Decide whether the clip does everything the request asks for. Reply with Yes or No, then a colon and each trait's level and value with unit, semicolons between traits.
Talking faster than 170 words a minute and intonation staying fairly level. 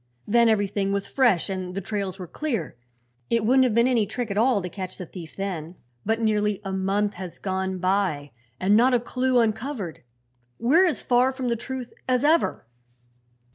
No: average, 185 wpm; average, 4.5 semitones